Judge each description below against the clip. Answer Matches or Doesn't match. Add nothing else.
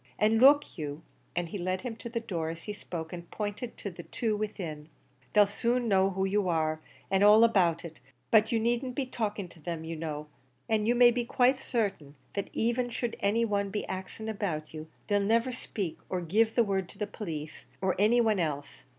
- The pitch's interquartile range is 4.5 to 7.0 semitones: Matches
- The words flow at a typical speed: Doesn't match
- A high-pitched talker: Matches